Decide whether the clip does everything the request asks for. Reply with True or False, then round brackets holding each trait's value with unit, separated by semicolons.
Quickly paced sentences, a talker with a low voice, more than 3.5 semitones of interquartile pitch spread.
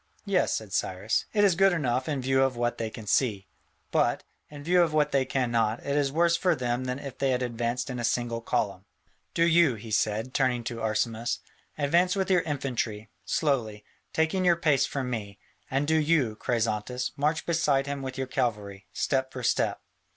False (195 wpm; 130 Hz; 4.3 semitones)